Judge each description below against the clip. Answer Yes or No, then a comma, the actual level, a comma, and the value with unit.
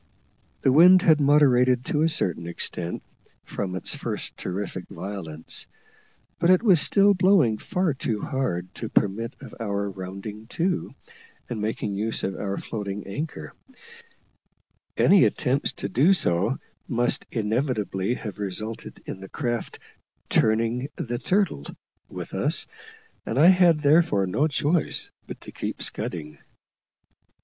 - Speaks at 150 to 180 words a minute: No, slow, 135 wpm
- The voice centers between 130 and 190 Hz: No, low, 115 Hz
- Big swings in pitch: Yes, wide, 7.3 semitones